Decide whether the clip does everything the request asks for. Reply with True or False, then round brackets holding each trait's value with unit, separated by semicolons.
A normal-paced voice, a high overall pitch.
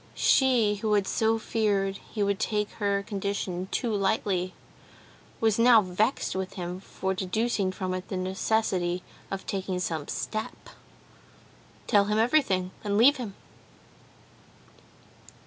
False (130 wpm; 200 Hz)